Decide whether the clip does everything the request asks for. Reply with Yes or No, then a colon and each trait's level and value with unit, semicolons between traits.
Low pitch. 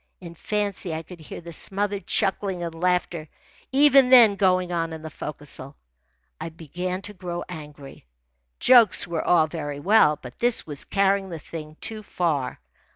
No: medium, 175 Hz